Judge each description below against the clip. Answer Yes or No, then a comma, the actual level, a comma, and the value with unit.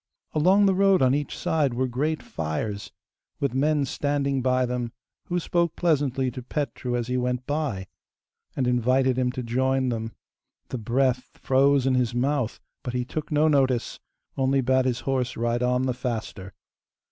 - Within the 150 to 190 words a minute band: Yes, average, 170 wpm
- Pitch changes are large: No, narrow, 2.5 semitones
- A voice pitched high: No, low, 130 Hz